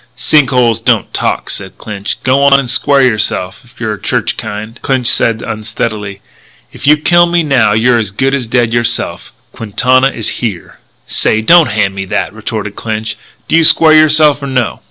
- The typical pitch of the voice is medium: No, low, 120 Hz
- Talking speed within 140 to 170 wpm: No, average, 185 wpm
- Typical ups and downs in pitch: Yes, average, 4.2 semitones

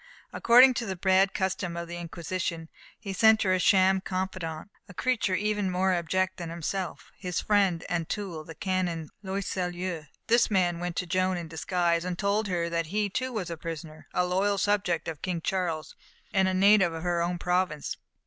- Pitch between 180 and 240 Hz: Yes, medium, 185 Hz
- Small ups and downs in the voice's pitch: Yes, narrow, 2.3 semitones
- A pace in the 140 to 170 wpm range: No, average, 185 wpm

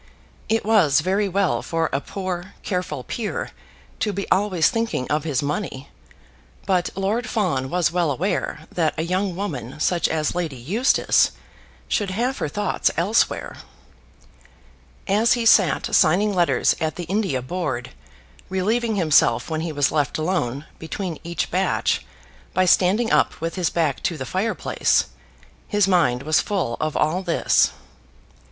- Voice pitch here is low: No, medium, 175 Hz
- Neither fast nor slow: Yes, average, 150 wpm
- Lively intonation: No, average, 4.6 semitones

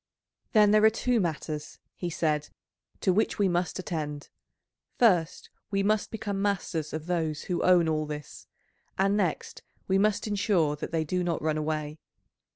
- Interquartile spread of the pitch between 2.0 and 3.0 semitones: No, average, 4.5 semitones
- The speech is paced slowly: No, average, 165 wpm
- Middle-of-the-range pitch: Yes, medium, 175 Hz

